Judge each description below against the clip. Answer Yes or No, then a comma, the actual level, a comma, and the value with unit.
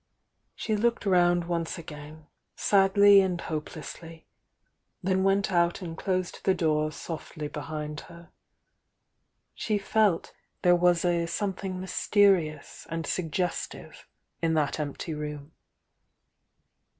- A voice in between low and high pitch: Yes, medium, 170 Hz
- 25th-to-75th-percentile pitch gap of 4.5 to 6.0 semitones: No, average, 3.3 semitones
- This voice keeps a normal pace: No, slow, 115 wpm